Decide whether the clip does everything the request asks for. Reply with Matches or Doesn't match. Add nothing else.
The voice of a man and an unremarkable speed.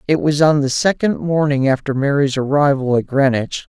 Matches